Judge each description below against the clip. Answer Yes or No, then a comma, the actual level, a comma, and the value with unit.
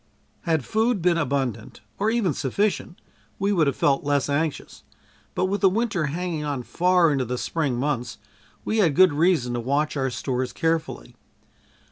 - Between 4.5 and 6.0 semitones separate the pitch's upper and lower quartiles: Yes, average, 5.2 semitones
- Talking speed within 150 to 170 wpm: Yes, average, 165 wpm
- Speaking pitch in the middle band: Yes, medium, 155 Hz